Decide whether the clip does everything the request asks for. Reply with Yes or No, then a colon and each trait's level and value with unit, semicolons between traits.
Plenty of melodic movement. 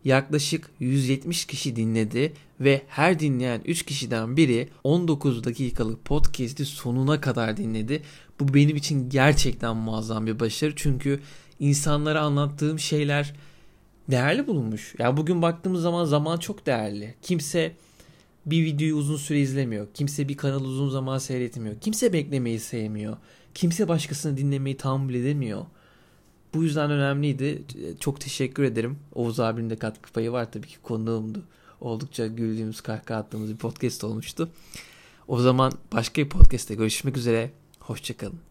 No: average, 4.5 semitones